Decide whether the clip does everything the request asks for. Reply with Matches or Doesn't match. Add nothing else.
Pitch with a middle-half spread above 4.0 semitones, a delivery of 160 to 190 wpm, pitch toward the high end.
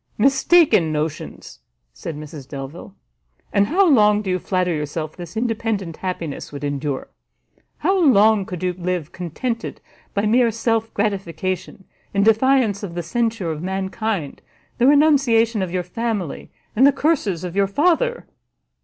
Doesn't match